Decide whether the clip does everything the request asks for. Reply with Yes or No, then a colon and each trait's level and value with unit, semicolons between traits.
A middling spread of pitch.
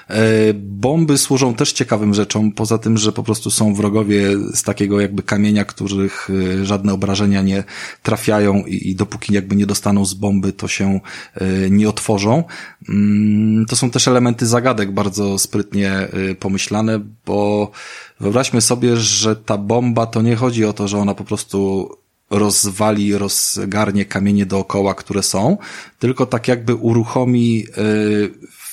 No: narrow, 2.0 semitones